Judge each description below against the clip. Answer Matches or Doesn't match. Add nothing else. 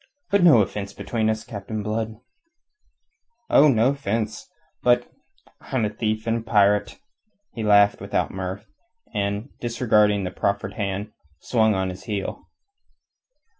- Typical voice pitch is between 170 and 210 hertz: Doesn't match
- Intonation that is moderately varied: Doesn't match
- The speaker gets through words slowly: Matches